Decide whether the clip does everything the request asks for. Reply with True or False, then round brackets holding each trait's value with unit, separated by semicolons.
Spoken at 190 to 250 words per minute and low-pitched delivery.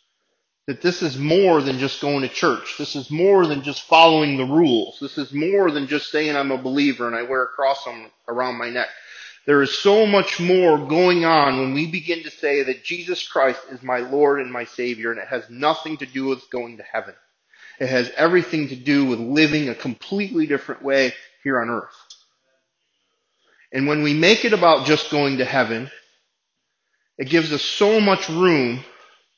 False (195 wpm; 145 Hz)